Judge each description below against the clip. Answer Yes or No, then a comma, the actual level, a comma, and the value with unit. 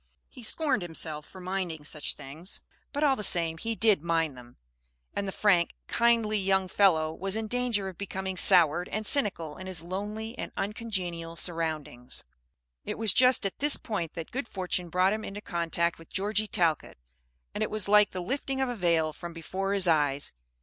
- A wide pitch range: No, average, 4.2 semitones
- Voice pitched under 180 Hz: No, high, 190 Hz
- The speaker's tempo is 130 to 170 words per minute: No, average, 185 wpm